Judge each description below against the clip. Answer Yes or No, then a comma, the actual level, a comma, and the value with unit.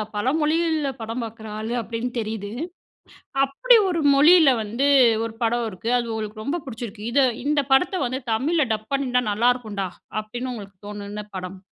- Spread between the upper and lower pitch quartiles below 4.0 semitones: No, average, 4.3 semitones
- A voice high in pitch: Yes, high, 235 Hz